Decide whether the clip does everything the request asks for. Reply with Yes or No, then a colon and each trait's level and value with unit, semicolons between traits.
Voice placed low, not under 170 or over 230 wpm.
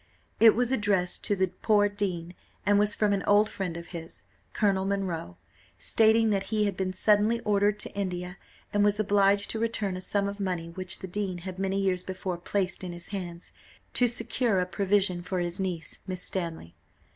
No: high, 195 Hz; average, 190 wpm